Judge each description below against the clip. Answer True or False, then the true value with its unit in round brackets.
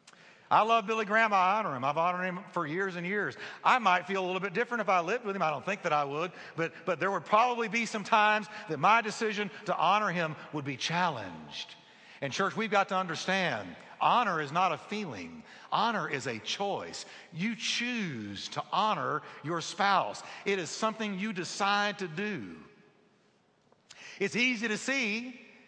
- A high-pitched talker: True (200 Hz)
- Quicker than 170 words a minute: True (190 wpm)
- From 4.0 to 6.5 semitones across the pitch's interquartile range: False (3.5 semitones)